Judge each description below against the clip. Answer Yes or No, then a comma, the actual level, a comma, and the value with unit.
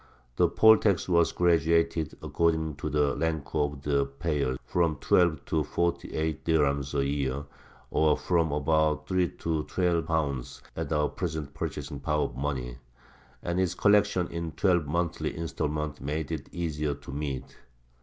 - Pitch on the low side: Yes, very low, 80 Hz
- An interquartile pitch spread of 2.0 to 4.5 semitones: Yes, average, 2.7 semitones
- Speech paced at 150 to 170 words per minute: Yes, average, 155 wpm